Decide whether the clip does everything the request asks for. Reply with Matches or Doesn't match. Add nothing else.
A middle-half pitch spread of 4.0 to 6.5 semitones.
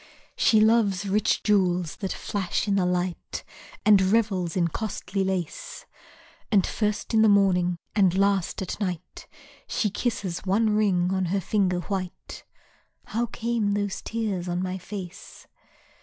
Doesn't match